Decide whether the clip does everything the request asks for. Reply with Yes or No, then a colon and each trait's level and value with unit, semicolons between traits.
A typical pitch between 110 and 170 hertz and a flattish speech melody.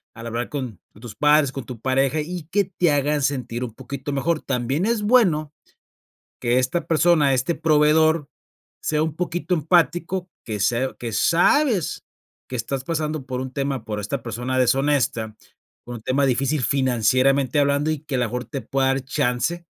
No: medium, 140 Hz; average, 3.8 semitones